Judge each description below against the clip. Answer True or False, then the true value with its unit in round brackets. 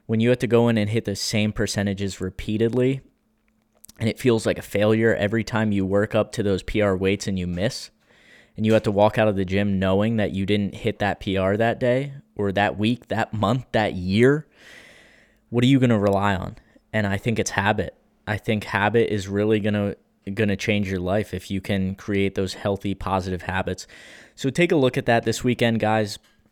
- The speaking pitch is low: True (105 Hz)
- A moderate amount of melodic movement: False (2.2 semitones)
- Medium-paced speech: False (215 wpm)